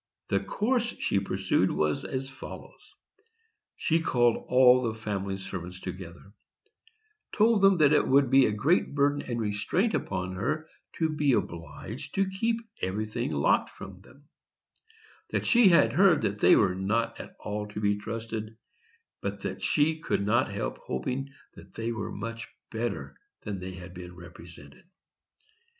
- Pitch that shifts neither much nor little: No, wide, 7.0 semitones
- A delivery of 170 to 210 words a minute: No, average, 155 wpm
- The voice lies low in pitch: Yes, low, 110 Hz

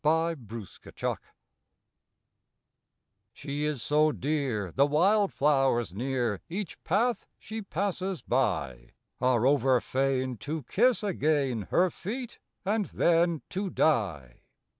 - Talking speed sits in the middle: No, slow, 100 wpm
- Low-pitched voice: No, medium, 150 Hz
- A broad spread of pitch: Yes, wide, 6.6 semitones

